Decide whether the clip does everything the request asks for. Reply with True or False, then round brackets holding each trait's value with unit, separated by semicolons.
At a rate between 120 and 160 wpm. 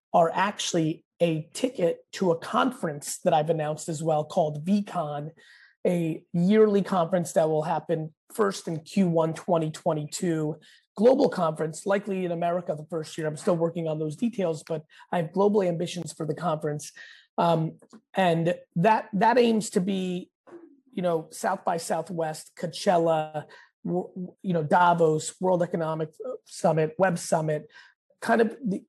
True (145 wpm)